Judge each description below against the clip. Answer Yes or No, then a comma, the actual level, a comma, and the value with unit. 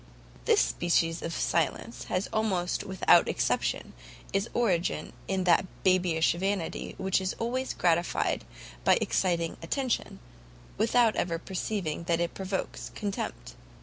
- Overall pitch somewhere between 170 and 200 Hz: Yes, medium, 185 Hz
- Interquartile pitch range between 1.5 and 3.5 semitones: Yes, average, 2.9 semitones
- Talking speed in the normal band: No, slow, 120 wpm